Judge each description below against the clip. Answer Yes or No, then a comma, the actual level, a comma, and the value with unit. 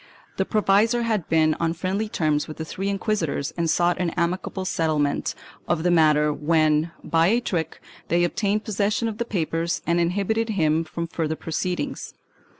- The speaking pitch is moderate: Yes, medium, 170 Hz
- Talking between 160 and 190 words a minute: Yes, average, 170 wpm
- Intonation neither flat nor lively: Yes, average, 4.0 semitones